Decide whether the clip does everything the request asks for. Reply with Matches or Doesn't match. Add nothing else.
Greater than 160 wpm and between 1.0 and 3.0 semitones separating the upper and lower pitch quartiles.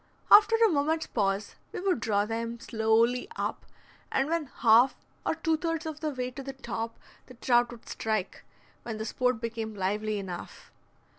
Doesn't match